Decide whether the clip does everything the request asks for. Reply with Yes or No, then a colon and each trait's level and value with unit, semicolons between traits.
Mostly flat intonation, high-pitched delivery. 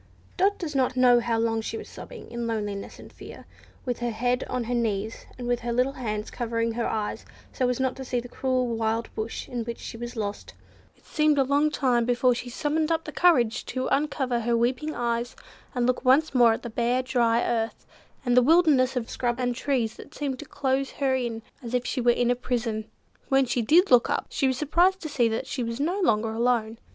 Yes: narrow, 2.3 semitones; high, 245 Hz